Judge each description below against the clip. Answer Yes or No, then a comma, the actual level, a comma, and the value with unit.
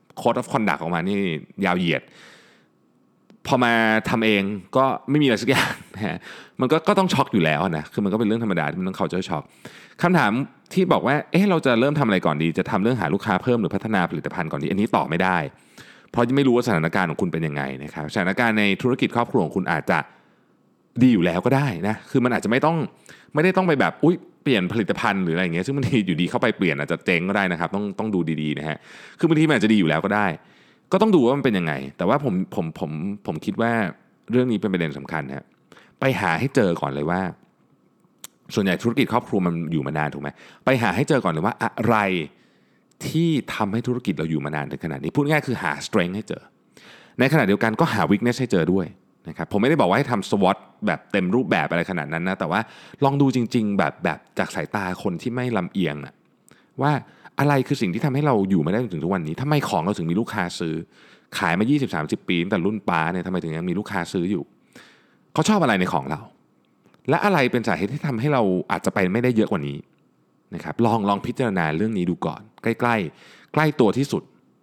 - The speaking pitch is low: Yes, low, 105 Hz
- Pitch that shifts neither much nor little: No, wide, 6.5 semitones